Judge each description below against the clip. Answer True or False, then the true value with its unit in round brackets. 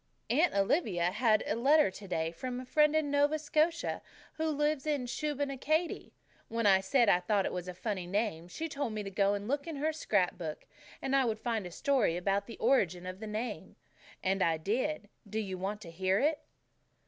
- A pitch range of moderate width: False (7.1 semitones)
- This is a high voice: True (220 Hz)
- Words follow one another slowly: False (200 wpm)